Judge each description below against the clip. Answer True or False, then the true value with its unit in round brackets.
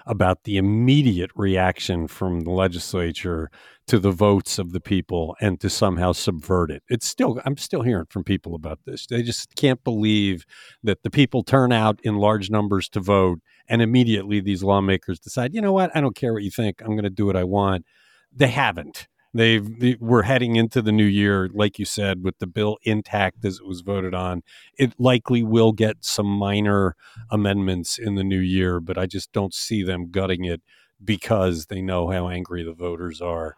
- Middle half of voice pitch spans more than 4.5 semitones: False (3.4 semitones)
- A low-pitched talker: True (100 Hz)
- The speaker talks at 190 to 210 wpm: True (200 wpm)